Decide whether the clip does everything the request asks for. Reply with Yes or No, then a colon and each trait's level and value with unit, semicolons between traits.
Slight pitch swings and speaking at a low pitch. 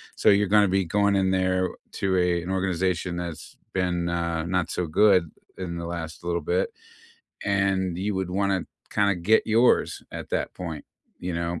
Yes: narrow, 2.2 semitones; very low, 90 Hz